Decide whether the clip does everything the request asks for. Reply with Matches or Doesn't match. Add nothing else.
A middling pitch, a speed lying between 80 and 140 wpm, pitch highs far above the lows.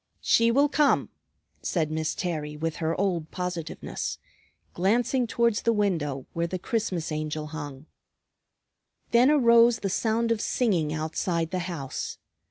Matches